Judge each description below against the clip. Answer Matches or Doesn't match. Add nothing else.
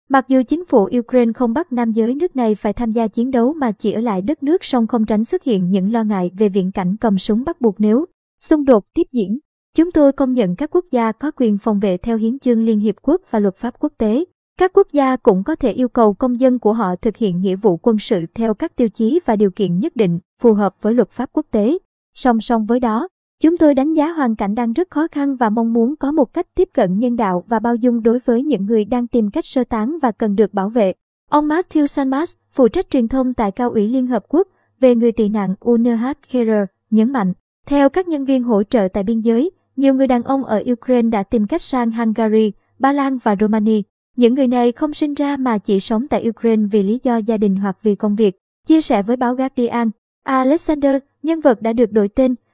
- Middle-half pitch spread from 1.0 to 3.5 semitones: Doesn't match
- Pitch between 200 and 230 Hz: Doesn't match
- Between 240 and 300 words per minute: Matches